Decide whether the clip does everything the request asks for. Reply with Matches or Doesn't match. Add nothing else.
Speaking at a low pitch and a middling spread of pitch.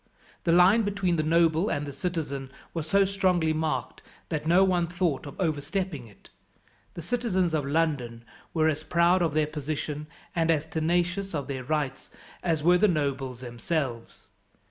Doesn't match